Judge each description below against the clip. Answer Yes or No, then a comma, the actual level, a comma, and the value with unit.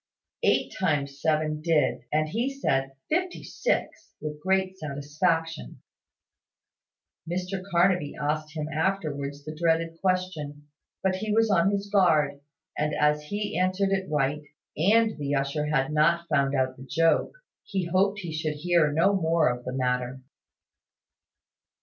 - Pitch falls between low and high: Yes, medium, 160 Hz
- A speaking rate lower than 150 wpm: Yes, average, 140 wpm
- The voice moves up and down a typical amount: Yes, average, 4.2 semitones